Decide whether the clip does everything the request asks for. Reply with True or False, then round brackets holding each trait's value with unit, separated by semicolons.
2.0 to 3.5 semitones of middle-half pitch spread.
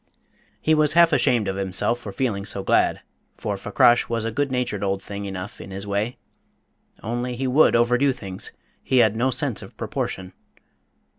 False (4.4 semitones)